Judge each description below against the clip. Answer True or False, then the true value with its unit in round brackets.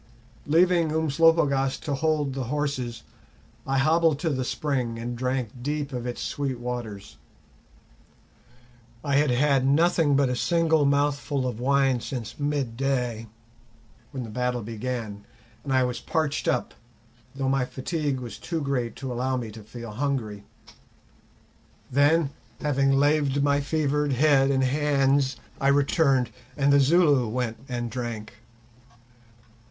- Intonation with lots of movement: False (2.8 semitones)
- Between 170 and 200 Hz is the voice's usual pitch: False (135 Hz)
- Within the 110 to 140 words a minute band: True (135 wpm)